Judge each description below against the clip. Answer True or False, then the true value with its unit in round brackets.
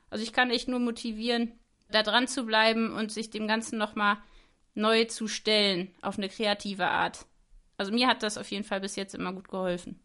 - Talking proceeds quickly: True (210 wpm)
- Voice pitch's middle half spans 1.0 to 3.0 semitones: True (2.5 semitones)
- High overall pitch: True (220 Hz)